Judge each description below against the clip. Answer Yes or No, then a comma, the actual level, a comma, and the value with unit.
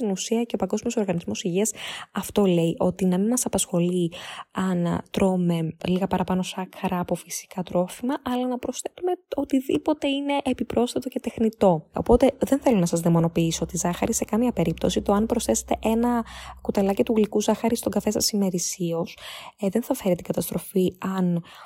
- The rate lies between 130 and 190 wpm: Yes, average, 165 wpm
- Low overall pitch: No, high, 200 Hz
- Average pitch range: Yes, average, 5.0 semitones